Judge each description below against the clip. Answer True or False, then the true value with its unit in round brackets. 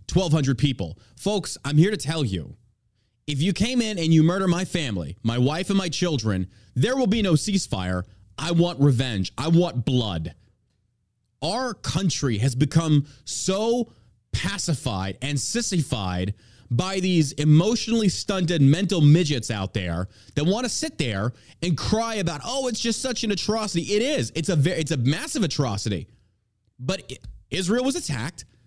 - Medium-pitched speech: True (150 Hz)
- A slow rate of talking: False (160 wpm)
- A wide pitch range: True (8.7 semitones)